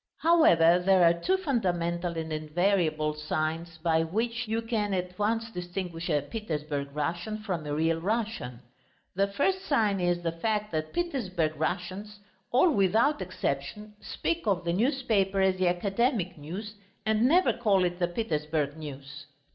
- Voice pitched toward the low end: No, medium, 180 Hz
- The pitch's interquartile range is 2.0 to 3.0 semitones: No, average, 4.9 semitones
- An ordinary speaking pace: Yes, average, 150 wpm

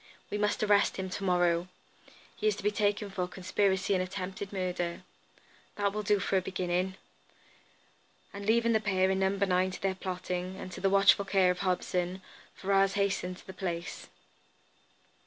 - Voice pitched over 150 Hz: Yes, high, 190 Hz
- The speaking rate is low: No, average, 175 wpm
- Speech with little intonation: Yes, narrow, 1.6 semitones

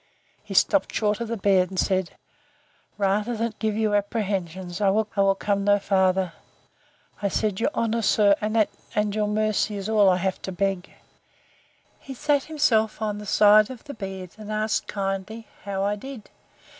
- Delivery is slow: No, average, 170 wpm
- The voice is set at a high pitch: Yes, high, 205 Hz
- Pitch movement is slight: Yes, narrow, 2.0 semitones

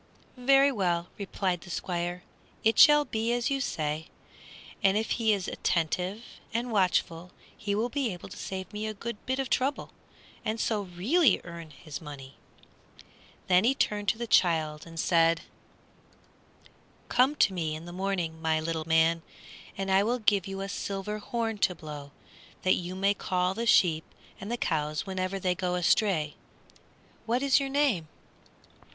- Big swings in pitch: No, average, 4.9 semitones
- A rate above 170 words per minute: No, average, 165 wpm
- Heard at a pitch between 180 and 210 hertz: Yes, high, 190 Hz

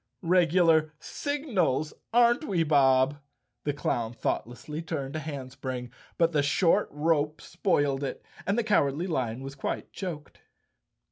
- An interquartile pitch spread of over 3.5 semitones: Yes, average, 4.3 semitones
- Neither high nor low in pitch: Yes, medium, 150 Hz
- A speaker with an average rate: No, slow, 130 wpm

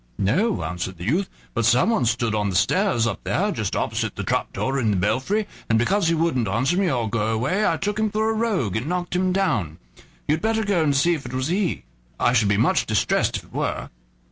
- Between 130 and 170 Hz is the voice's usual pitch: Yes, low, 135 Hz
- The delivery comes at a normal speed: No, fast, 235 wpm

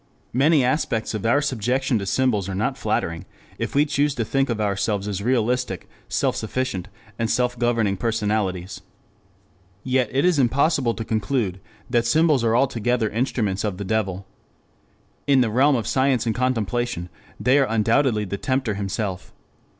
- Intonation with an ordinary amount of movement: Yes, average, 4.0 semitones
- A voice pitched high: No, low, 115 Hz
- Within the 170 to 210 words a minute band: No, average, 160 wpm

